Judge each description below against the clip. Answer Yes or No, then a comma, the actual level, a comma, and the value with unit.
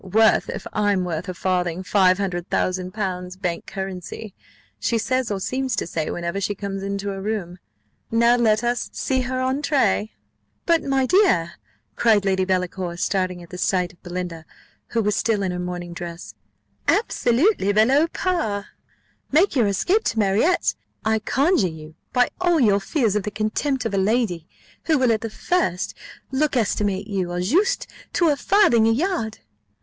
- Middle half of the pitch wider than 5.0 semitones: Yes, wide, 5.6 semitones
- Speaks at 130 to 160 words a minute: No, average, 175 wpm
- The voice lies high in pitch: Yes, high, 205 Hz